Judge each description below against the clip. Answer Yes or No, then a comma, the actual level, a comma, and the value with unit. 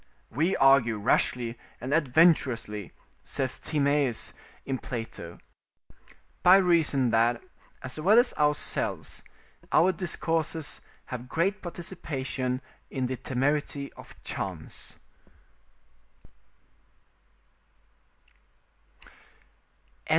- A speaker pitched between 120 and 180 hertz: Yes, medium, 140 Hz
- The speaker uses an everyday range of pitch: Yes, average, 4.6 semitones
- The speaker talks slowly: Yes, slow, 75 wpm